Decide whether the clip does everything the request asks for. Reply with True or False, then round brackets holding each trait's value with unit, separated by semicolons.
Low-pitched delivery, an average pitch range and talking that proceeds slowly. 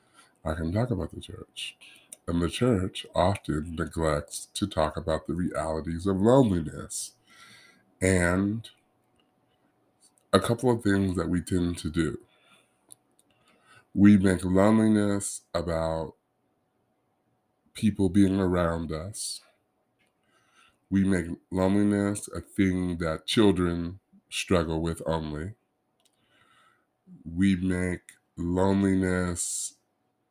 True (90 Hz; 3.1 semitones; 95 wpm)